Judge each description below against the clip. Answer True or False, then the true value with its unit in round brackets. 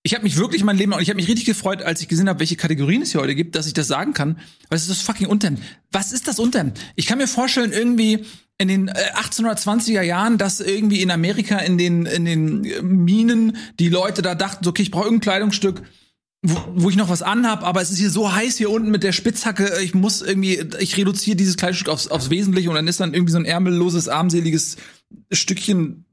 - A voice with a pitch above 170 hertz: True (190 Hz)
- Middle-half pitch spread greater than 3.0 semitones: True (3.4 semitones)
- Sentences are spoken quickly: True (230 wpm)